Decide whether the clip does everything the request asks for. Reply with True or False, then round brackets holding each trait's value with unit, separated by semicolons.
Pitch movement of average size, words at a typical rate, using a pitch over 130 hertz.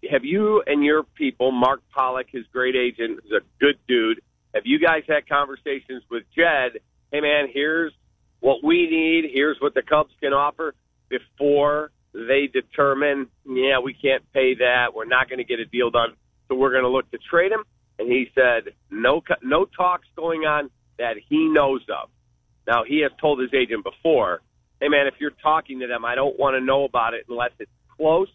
True (3.4 semitones; 195 wpm; 140 Hz)